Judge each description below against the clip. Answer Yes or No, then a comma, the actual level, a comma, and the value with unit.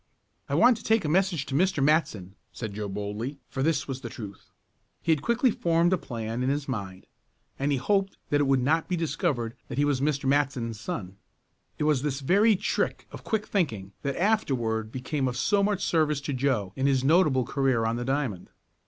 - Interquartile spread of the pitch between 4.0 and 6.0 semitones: Yes, wide, 5.4 semitones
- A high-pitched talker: No, medium, 140 Hz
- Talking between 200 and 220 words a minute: Yes, fast, 205 wpm